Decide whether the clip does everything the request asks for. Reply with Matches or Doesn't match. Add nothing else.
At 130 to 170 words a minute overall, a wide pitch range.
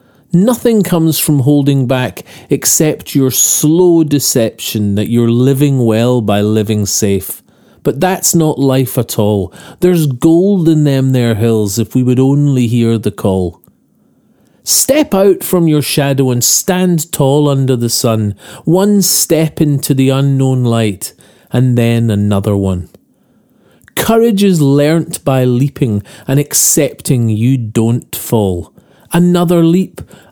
Matches